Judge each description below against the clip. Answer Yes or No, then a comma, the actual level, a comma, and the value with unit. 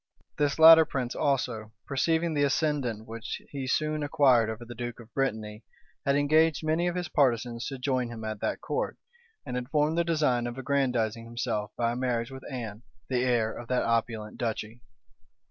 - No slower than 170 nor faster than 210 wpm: Yes, average, 180 wpm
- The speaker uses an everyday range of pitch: Yes, average, 3.8 semitones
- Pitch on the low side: Yes, low, 125 Hz